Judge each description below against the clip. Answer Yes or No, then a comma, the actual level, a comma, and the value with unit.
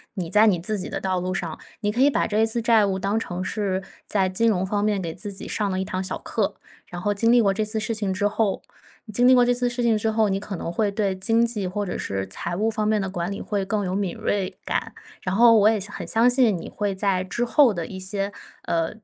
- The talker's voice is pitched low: No, high, 205 Hz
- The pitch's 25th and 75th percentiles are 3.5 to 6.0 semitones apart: No, average, 2.8 semitones